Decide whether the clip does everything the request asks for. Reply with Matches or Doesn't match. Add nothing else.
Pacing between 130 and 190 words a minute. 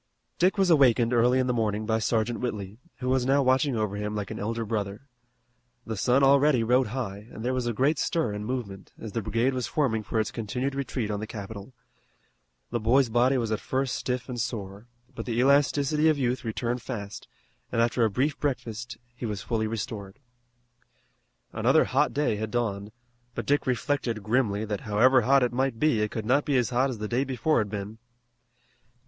Doesn't match